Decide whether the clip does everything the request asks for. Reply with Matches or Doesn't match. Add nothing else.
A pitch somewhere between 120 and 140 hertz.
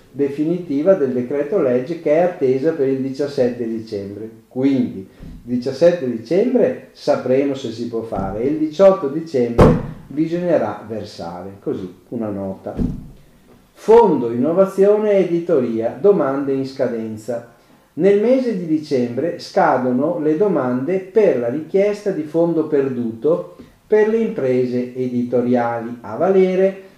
Matches